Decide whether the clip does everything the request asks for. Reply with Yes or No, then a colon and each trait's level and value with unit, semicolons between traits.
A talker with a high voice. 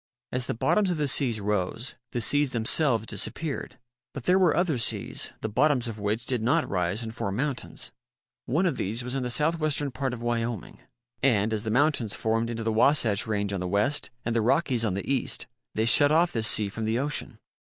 No: low, 120 Hz